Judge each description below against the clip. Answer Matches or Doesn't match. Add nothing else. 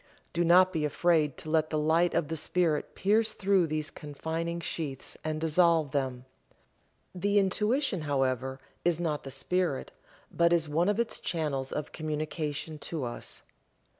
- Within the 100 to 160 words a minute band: Matches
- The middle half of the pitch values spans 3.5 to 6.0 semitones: Doesn't match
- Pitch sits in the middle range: Matches